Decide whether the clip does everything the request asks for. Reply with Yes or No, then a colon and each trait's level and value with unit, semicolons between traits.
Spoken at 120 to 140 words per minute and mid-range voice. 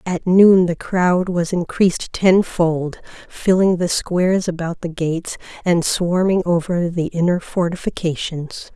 Yes: slow, 135 wpm; medium, 175 Hz